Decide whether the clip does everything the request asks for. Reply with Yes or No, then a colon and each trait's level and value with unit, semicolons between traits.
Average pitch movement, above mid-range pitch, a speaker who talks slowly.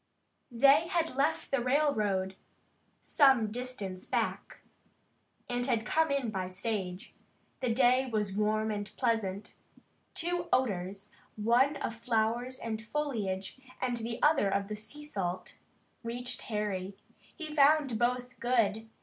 Yes: average, 4.2 semitones; high, 230 Hz; slow, 125 wpm